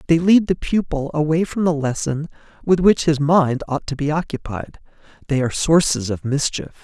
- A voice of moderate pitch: Yes, medium, 155 Hz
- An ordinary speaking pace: Yes, average, 185 wpm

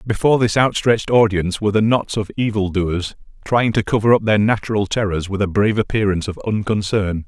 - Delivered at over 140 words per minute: Yes, average, 190 wpm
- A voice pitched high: No, low, 105 Hz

